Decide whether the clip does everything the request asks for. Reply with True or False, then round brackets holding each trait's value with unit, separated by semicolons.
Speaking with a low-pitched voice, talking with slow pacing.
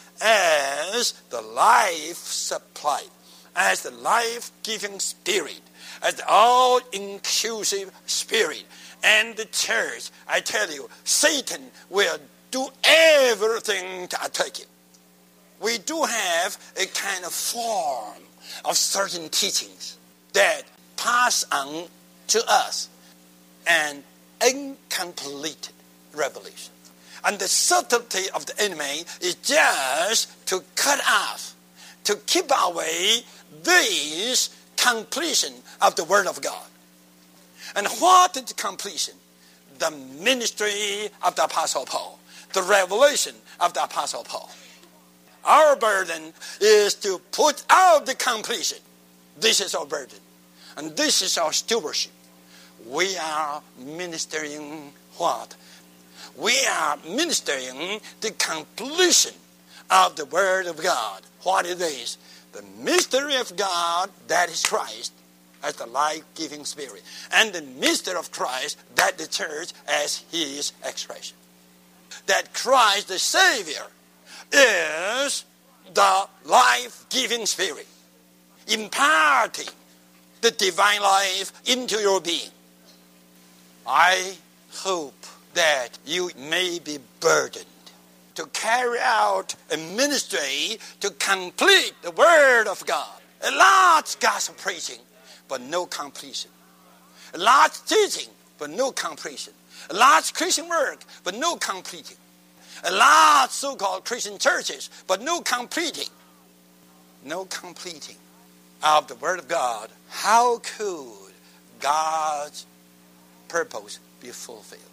False (165 Hz; 110 wpm)